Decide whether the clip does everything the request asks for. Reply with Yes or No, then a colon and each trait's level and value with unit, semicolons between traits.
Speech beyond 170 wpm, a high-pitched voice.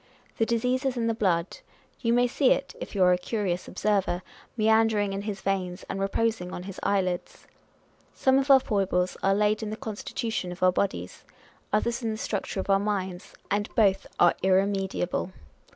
Yes: average, 185 wpm; high, 200 Hz